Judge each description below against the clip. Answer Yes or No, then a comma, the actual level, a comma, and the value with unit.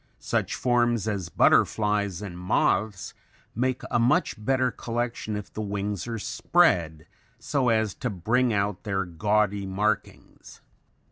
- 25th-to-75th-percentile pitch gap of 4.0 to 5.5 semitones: No, average, 3.4 semitones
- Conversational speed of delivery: No, slow, 130 wpm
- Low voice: Yes, low, 105 Hz